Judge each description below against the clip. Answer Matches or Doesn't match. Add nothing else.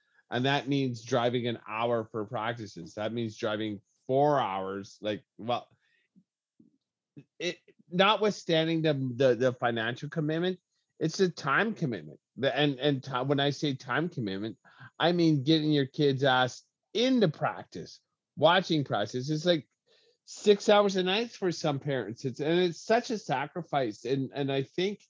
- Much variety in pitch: Matches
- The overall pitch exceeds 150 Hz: Doesn't match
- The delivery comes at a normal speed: Matches